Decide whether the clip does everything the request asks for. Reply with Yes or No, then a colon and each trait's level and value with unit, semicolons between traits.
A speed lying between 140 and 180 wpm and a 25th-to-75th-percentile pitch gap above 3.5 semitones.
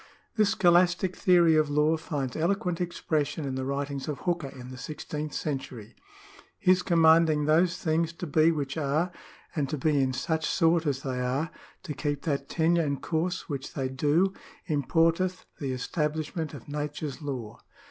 No: average, 170 wpm; average, 3.2 semitones